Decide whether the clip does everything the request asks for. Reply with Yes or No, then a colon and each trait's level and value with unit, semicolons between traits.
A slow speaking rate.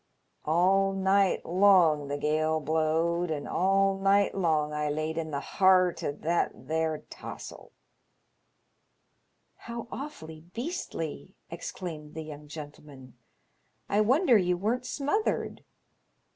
Yes: slow, 125 wpm